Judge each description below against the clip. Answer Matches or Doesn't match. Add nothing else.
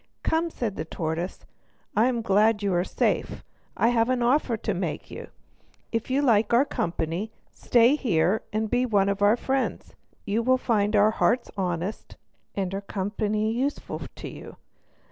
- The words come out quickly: Doesn't match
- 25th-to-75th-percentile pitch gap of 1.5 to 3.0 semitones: Doesn't match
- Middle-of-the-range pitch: Doesn't match